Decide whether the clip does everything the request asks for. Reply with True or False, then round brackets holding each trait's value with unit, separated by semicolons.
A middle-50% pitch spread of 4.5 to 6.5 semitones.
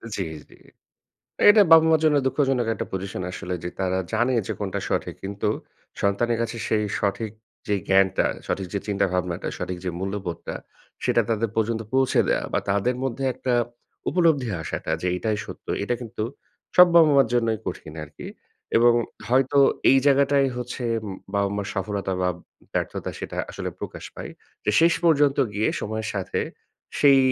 True (5.4 semitones)